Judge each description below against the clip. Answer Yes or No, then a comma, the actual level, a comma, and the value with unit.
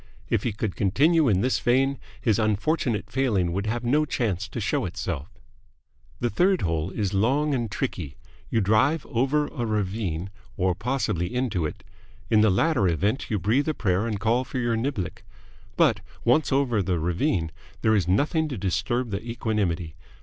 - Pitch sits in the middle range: No, low, 110 Hz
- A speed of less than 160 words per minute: No, average, 170 wpm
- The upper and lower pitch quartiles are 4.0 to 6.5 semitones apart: Yes, wide, 5.4 semitones